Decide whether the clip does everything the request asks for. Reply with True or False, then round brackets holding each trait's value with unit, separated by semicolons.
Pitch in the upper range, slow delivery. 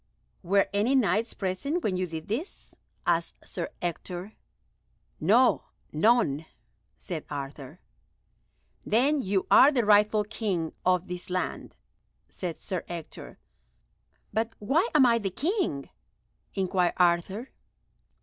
True (195 Hz; 115 wpm)